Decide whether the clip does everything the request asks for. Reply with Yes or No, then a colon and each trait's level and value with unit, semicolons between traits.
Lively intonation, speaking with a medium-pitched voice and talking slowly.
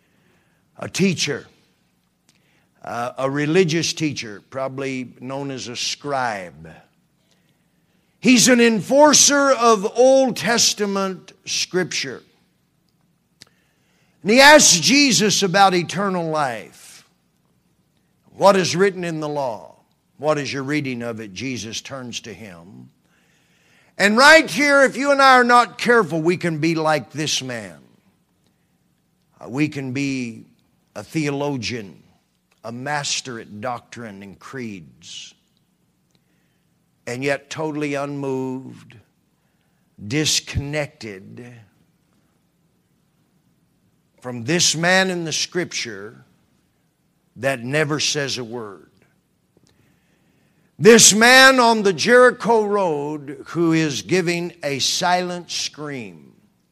Yes: wide, 7.0 semitones; medium, 155 Hz; slow, 105 wpm